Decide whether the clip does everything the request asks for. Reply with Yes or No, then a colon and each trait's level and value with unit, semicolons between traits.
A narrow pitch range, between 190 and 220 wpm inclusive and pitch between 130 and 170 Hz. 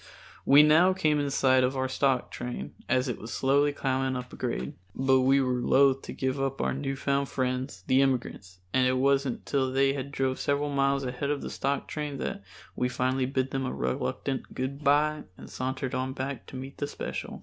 Yes: narrow, 1.4 semitones; fast, 205 wpm; low, 135 Hz